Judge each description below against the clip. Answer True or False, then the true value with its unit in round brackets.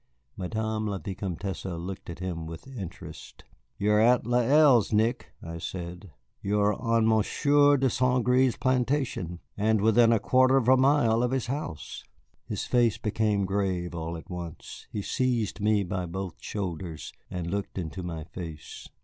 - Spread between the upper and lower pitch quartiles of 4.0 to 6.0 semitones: True (5.3 semitones)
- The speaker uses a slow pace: False (165 wpm)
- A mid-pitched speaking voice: False (105 Hz)